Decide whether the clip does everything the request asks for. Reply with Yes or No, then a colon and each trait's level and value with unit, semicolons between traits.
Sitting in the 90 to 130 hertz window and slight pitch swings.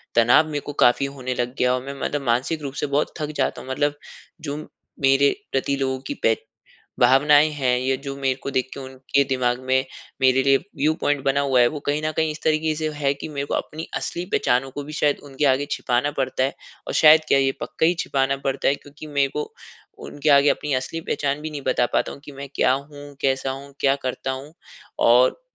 No: medium, 140 Hz; narrow, 1.9 semitones